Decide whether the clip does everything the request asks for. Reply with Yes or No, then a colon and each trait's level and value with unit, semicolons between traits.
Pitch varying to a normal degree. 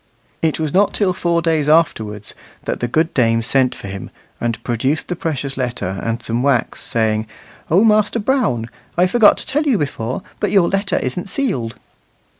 No: wide, 7.9 semitones